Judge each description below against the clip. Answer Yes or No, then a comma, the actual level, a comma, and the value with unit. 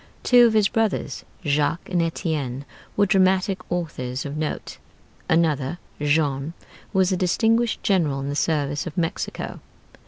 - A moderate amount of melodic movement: Yes, average, 4.8 semitones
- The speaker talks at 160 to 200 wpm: No, slow, 135 wpm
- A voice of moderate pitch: Yes, medium, 165 Hz